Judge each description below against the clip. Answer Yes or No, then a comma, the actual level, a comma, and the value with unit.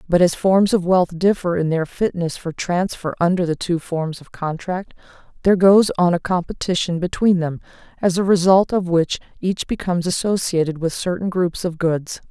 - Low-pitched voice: No, medium, 175 Hz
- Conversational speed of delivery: Yes, average, 180 wpm